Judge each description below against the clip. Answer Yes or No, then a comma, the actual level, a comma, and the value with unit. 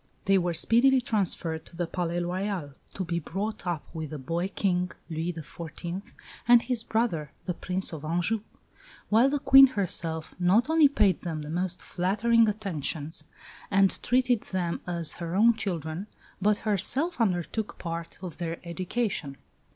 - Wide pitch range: No, average, 4.6 semitones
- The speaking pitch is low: No, medium, 180 Hz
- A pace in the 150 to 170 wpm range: Yes, average, 155 wpm